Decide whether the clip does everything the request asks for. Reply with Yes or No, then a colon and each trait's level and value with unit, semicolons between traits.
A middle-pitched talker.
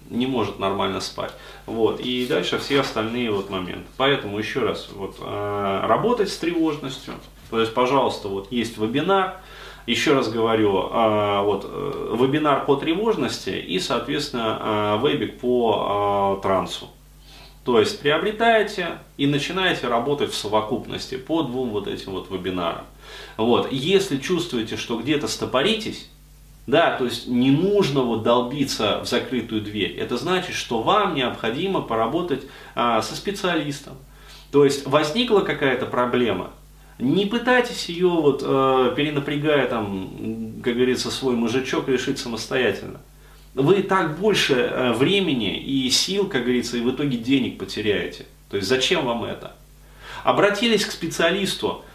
No: low, 130 Hz